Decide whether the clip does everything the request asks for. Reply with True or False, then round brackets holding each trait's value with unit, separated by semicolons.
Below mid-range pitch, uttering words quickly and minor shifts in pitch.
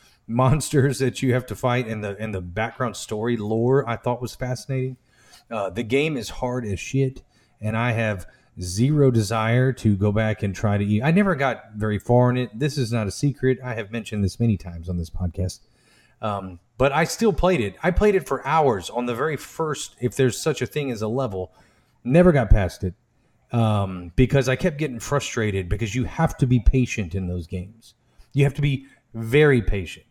False (120 Hz; 210 wpm; 4.0 semitones)